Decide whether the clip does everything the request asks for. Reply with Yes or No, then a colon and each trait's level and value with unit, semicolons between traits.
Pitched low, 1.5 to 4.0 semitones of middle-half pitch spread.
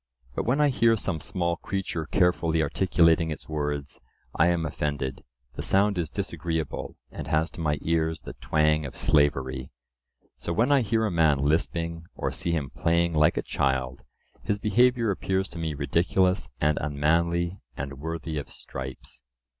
Yes: very low, 80 Hz; average, 3.2 semitones